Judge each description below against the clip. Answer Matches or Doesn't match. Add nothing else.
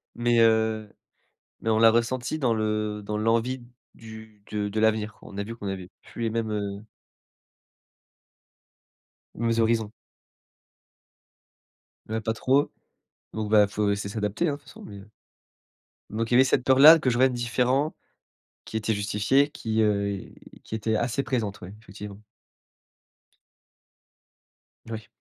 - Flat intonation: Matches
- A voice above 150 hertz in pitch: Doesn't match